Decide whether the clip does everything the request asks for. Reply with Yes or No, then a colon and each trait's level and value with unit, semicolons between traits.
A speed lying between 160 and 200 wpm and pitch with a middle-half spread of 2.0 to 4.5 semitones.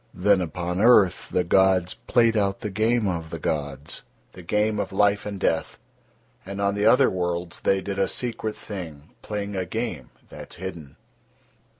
Yes: average, 175 wpm; average, 3.1 semitones